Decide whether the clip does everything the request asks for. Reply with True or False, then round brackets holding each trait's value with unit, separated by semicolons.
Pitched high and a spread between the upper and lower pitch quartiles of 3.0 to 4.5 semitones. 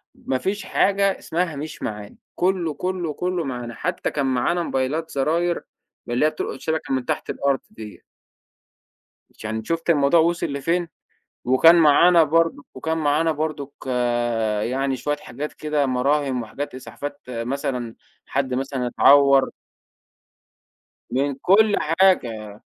False (145 Hz; 4.1 semitones)